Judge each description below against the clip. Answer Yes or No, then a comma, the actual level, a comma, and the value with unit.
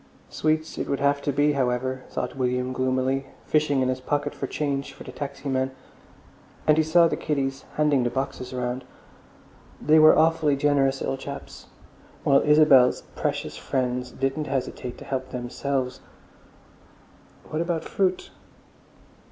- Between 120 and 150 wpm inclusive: Yes, average, 140 wpm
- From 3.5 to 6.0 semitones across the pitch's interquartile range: No, narrow, 2.5 semitones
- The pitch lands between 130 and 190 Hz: Yes, low, 135 Hz